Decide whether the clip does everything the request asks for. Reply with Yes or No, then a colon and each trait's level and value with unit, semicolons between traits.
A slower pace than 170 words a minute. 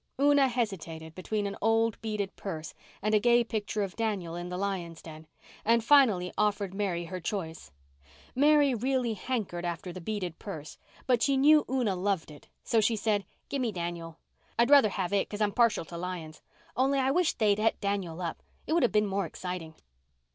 No: average, 190 wpm